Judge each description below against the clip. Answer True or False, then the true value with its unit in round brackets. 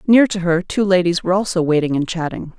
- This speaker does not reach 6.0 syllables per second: False (6.3 syllables/s)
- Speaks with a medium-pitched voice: True (180 Hz)